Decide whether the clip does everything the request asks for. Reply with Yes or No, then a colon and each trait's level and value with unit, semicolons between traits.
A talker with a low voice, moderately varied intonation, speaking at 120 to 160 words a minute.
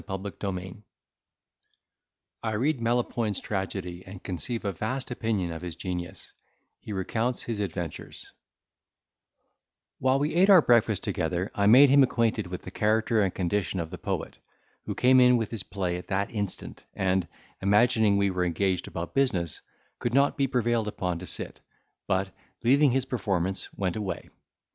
Yes: low, 100 Hz; average, 4.5 semitones; average, 155 wpm